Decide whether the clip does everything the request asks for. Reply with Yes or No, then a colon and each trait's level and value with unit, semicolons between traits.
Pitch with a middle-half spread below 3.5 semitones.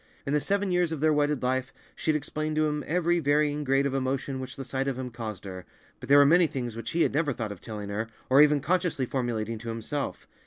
No: average, 3.8 semitones